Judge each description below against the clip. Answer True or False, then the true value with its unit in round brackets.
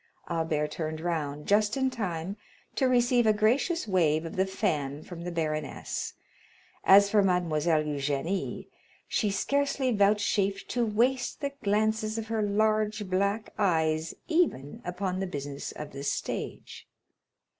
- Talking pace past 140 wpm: False (135 wpm)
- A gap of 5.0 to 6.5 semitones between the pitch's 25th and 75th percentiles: True (5.3 semitones)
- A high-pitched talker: True (195 Hz)